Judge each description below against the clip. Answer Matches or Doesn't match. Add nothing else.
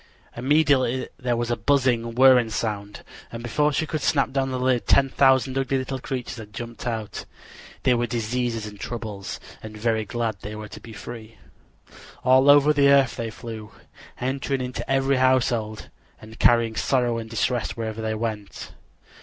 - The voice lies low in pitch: Matches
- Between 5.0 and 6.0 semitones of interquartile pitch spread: Doesn't match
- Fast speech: Doesn't match